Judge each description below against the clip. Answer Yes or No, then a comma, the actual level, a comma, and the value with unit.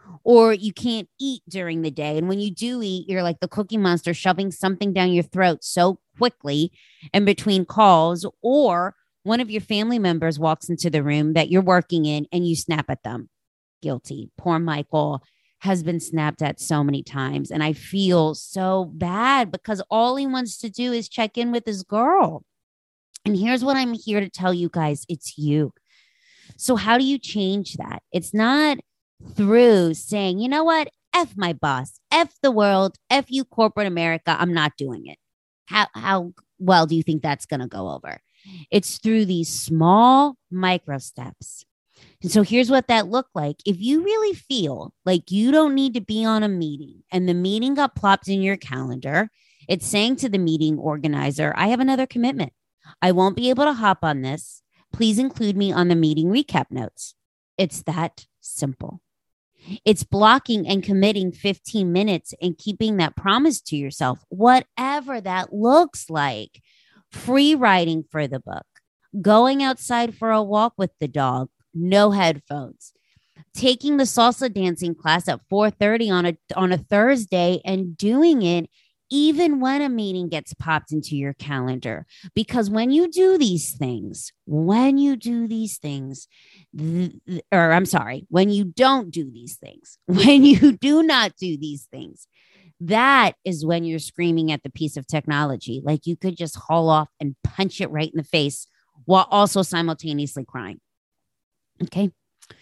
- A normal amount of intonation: No, wide, 6.0 semitones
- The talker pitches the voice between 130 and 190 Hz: Yes, medium, 185 Hz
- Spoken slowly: No, average, 175 wpm